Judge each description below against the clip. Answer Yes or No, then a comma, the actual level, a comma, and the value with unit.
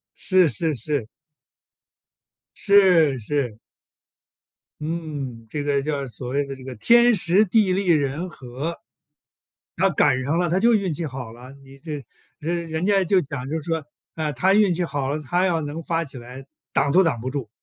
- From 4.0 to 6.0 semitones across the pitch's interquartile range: Yes, average, 4.5 semitones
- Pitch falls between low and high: Yes, medium, 150 Hz